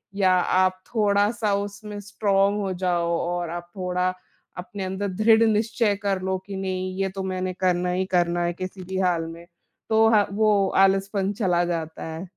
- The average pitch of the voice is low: No, high, 190 Hz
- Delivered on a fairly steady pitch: Yes, narrow, 2.1 semitones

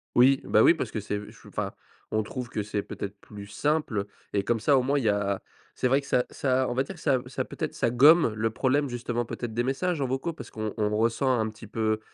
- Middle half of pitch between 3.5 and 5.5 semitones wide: Yes, average, 3.9 semitones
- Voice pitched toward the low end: Yes, low, 120 Hz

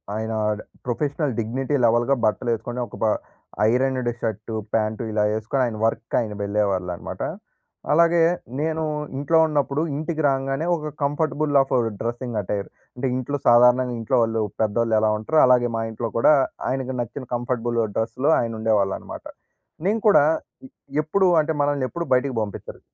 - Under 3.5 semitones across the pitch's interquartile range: No, average, 4.3 semitones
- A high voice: No, low, 125 Hz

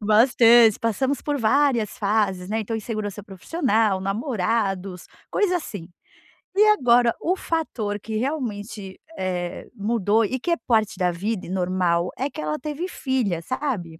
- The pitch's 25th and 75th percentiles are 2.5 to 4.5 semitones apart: No, average, 5.0 semitones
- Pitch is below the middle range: No, high, 220 Hz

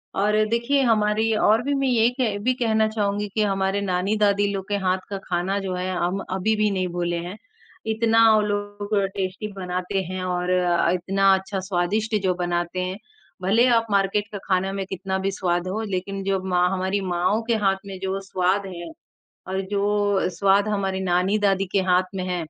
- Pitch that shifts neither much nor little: No, narrow, 2.2 semitones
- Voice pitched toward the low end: No, high, 195 Hz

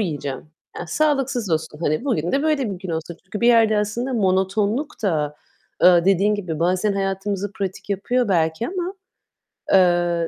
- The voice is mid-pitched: No, high, 195 Hz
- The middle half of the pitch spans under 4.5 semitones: No, average, 4.8 semitones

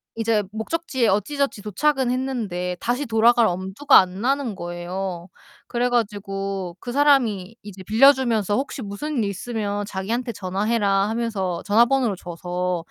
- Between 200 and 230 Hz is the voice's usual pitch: Yes, high, 215 Hz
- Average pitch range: Yes, average, 4.3 semitones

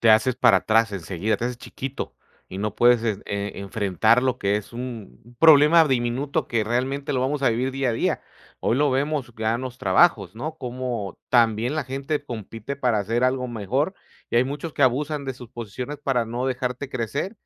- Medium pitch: No, low, 125 Hz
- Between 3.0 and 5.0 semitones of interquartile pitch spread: Yes, average, 3.4 semitones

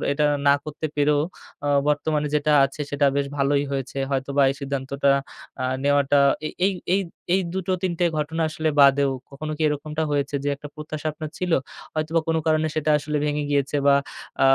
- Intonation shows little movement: Yes, narrow, 1.7 semitones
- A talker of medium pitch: Yes, medium, 145 Hz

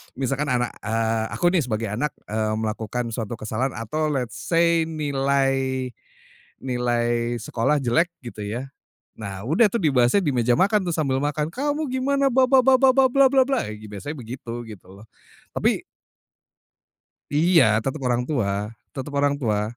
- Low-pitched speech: Yes, low, 130 Hz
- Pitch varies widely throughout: Yes, wide, 6.2 semitones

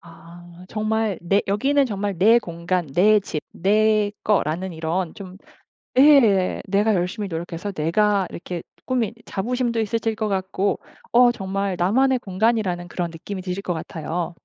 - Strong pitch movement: No, average, 3.6 semitones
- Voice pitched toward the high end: Yes, high, 195 Hz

